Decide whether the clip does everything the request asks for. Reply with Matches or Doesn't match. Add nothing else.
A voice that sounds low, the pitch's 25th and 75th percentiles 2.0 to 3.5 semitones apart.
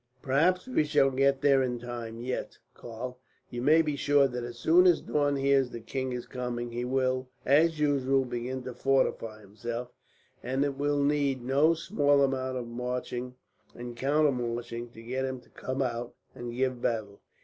Matches